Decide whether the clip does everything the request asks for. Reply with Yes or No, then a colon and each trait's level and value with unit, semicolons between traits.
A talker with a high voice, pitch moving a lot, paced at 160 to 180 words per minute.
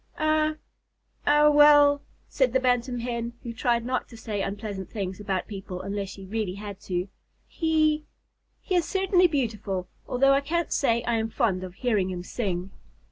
Yes: high, 235 Hz; wide, 6.6 semitones; average, 175 wpm